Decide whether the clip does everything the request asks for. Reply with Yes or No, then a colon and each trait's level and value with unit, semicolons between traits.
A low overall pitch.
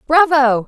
No: very high, 285 Hz